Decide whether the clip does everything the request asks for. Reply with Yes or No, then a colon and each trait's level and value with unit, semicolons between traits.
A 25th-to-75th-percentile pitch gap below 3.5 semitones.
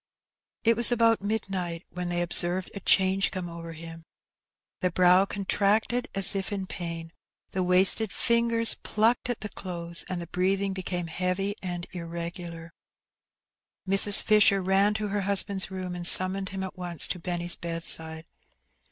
Yes: narrow, 2.4 semitones